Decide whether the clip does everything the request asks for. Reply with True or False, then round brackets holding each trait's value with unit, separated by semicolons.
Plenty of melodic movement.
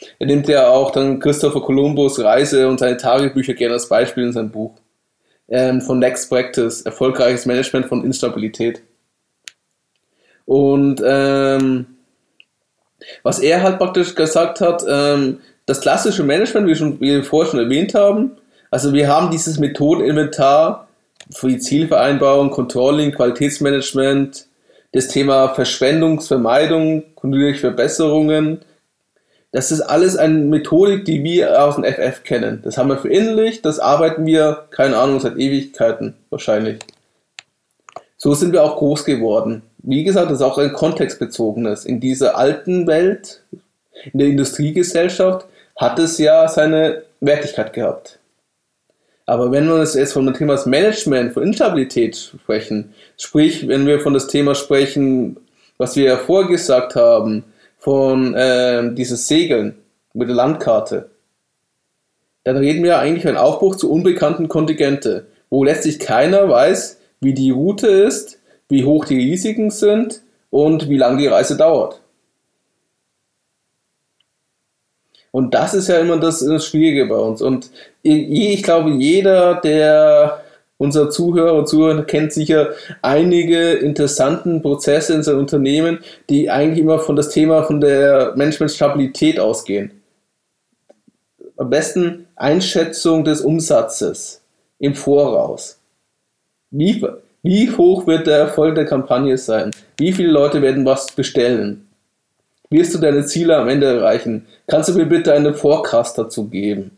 False (3.4 semitones)